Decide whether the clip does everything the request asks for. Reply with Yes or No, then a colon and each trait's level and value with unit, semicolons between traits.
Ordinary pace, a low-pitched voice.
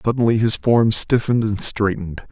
Yes: average, 155 wpm; low, 110 Hz